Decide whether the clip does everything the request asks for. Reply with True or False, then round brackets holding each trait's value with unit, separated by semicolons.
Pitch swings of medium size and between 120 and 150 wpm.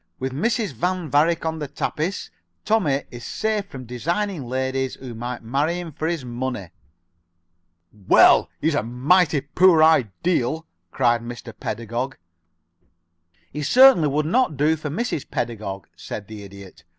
False (5.7 semitones; 140 wpm)